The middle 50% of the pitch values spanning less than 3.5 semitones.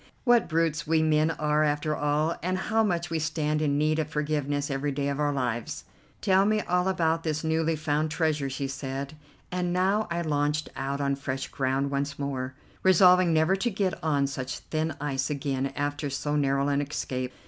Yes: average, 2.7 semitones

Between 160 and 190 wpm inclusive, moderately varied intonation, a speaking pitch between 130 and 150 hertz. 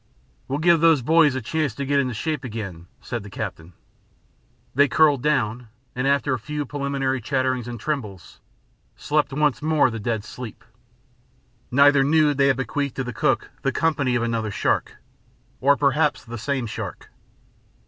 Yes: average, 165 wpm; average, 3.6 semitones; low, 135 Hz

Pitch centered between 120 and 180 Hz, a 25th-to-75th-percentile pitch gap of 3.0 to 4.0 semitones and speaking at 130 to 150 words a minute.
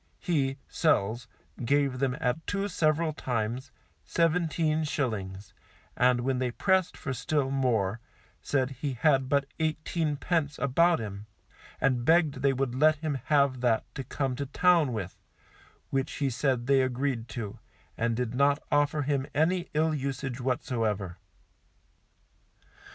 Yes: low, 135 Hz; average, 3.7 semitones; average, 140 wpm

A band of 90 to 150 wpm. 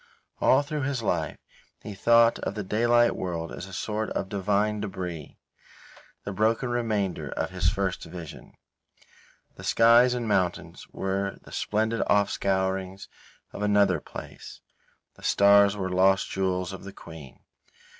Yes: average, 145 wpm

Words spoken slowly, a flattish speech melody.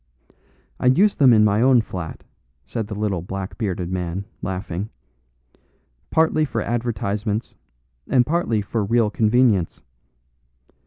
No: slow, 120 wpm; average, 3.9 semitones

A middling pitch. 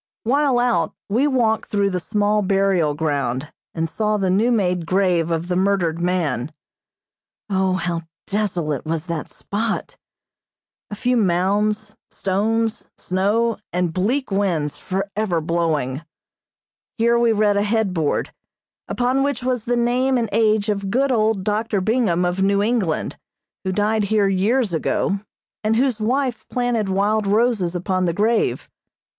No: high, 200 Hz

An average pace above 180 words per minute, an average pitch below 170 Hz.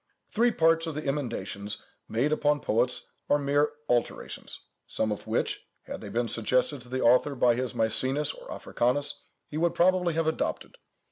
No: average, 165 wpm; medium, 140 Hz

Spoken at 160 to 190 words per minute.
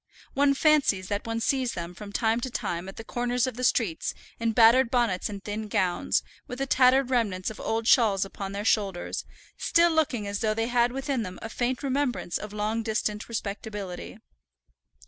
Yes: average, 185 wpm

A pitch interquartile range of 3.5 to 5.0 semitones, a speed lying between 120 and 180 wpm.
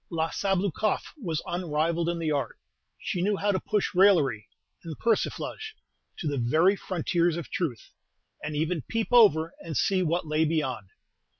Yes: average, 3.9 semitones; average, 160 wpm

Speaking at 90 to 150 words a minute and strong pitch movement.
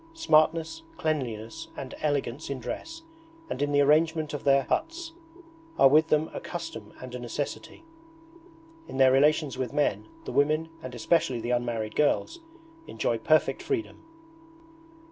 No: average, 145 wpm; average, 3.8 semitones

